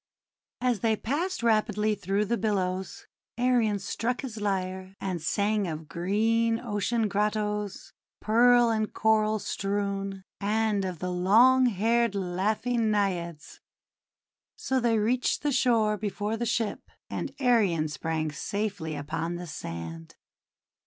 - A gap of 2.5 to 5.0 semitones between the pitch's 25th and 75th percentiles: Yes, average, 3.4 semitones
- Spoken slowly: Yes, slow, 125 wpm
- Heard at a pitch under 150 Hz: No, high, 210 Hz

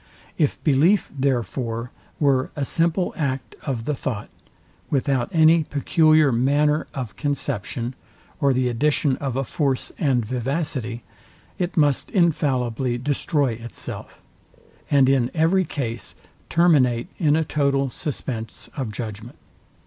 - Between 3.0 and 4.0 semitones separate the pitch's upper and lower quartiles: Yes, average, 3.6 semitones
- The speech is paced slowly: Yes, slow, 120 wpm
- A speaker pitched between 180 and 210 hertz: No, low, 135 Hz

